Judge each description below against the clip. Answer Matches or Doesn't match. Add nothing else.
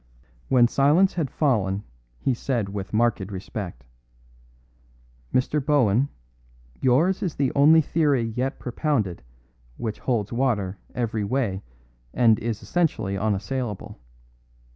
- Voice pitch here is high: Doesn't match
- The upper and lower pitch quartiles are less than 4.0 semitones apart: Doesn't match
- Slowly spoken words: Matches